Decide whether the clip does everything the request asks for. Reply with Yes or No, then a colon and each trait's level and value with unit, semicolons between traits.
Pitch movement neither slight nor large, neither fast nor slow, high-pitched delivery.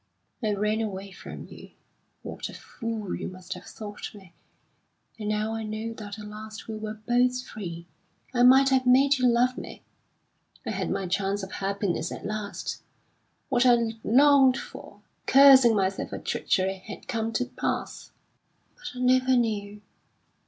Yes: average, 3.6 semitones; average, 160 wpm; high, 220 Hz